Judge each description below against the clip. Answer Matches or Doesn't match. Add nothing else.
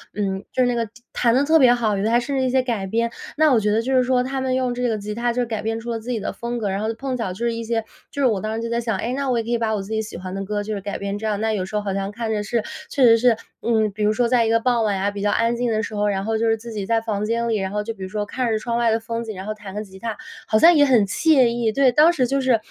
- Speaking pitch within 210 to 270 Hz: Matches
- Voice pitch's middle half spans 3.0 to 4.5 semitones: Doesn't match